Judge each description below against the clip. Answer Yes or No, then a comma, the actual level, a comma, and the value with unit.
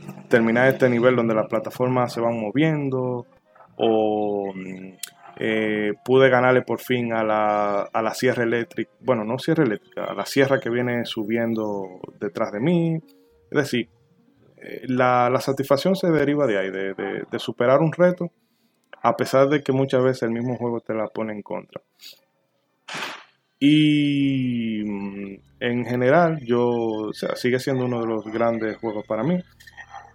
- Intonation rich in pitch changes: No, average, 3.5 semitones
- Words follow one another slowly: No, average, 155 wpm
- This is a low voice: Yes, low, 120 Hz